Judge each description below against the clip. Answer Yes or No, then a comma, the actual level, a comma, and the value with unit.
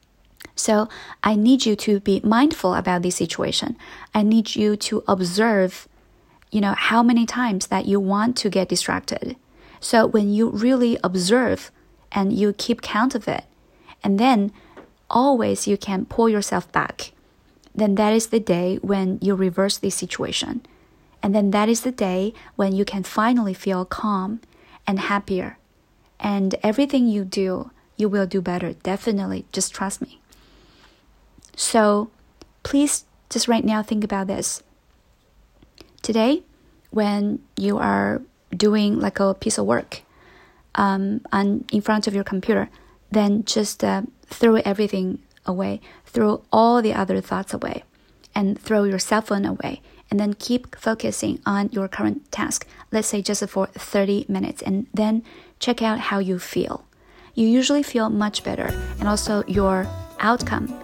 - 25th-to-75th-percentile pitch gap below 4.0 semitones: Yes, narrow, 2.5 semitones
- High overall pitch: Yes, high, 210 Hz